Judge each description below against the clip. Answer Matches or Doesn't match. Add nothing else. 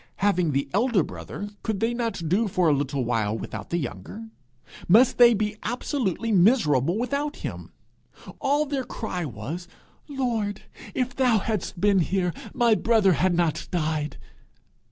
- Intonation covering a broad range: Matches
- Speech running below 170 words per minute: Matches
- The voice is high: Matches